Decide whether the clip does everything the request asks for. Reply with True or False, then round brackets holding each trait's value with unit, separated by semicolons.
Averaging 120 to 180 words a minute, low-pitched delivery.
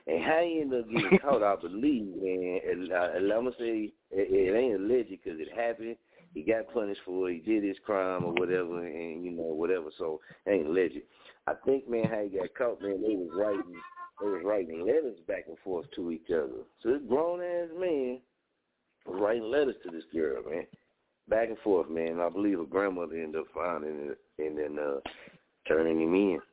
False (205 wpm; 115 Hz)